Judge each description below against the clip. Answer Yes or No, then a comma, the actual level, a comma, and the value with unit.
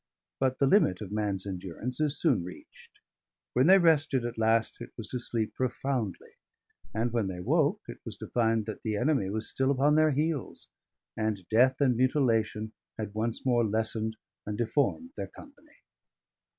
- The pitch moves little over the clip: No, average, 4.0 semitones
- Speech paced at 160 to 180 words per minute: Yes, average, 170 wpm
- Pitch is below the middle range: Yes, low, 115 Hz